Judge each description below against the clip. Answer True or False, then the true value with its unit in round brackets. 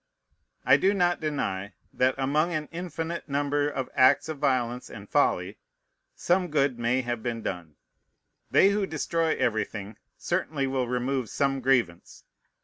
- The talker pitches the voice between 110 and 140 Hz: True (135 Hz)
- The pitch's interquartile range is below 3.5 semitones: False (4.5 semitones)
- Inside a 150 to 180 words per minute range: False (140 wpm)